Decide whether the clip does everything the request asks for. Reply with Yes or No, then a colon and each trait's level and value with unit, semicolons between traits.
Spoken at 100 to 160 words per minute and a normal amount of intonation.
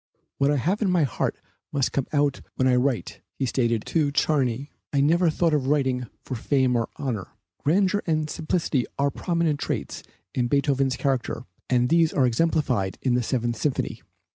No: average, 175 wpm; average, 3.6 semitones